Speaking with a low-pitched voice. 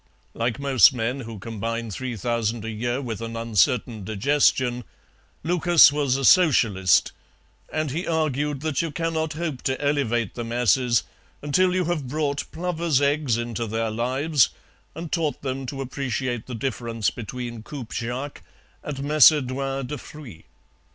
Yes: low, 130 Hz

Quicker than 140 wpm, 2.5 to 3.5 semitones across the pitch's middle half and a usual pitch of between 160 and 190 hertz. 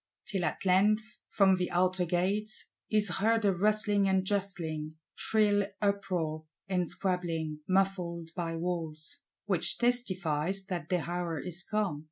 No: slow, 135 wpm; average, 2.9 semitones; medium, 185 Hz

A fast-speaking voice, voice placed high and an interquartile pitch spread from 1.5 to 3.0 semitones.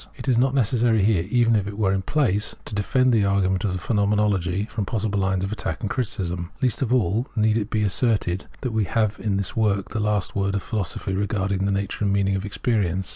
No: fast, 230 wpm; low, 105 Hz; narrow, 2.5 semitones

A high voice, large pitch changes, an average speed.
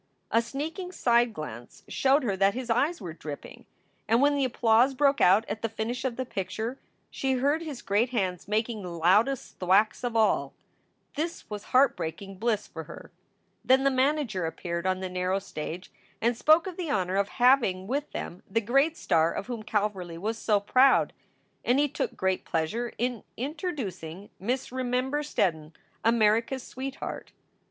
Yes: high, 230 Hz; wide, 5.7 semitones; average, 175 wpm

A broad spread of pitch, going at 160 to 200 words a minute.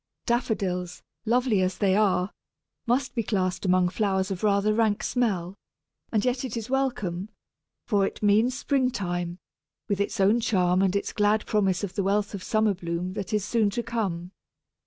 No: average, 3.4 semitones; average, 175 wpm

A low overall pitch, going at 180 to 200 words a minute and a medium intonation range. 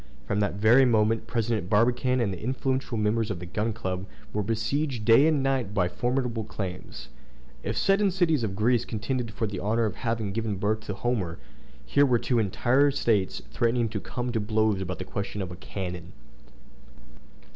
Yes: low, 110 Hz; average, 185 wpm; average, 3.4 semitones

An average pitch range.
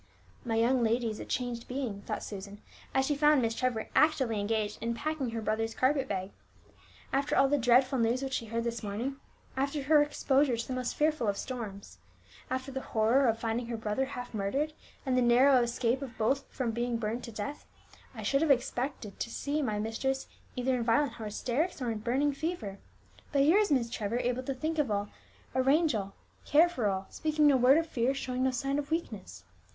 Yes: average, 3.4 semitones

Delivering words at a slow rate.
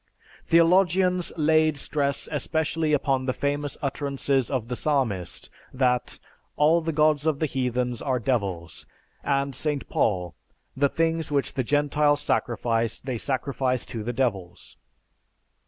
Yes: slow, 130 wpm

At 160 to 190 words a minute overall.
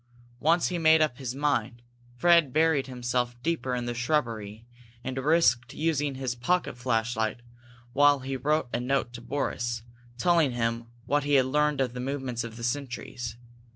Yes: average, 170 wpm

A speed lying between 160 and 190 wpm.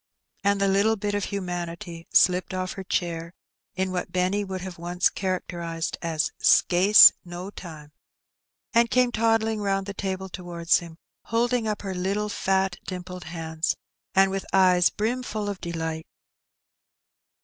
No: average, 145 wpm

